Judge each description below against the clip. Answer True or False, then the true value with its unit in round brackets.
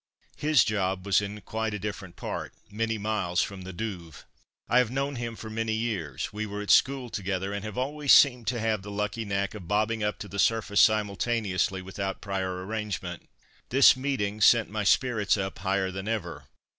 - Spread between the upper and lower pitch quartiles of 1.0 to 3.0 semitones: True (2.6 semitones)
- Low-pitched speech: True (105 Hz)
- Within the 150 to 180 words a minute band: False (190 wpm)